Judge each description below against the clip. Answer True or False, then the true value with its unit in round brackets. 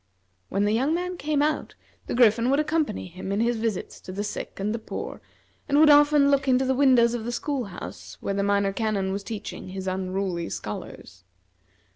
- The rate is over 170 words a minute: True (200 wpm)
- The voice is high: True (225 Hz)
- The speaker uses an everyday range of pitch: False (6.0 semitones)